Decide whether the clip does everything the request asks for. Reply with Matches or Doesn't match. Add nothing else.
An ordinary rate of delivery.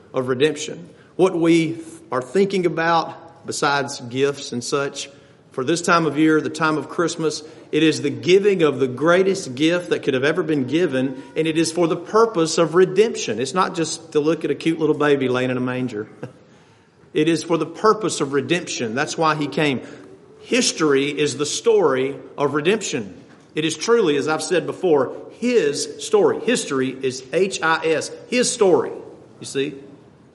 Matches